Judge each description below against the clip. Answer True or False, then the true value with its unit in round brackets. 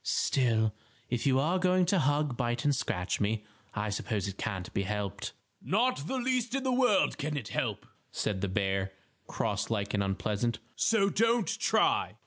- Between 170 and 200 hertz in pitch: False (120 Hz)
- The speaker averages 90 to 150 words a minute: False (180 wpm)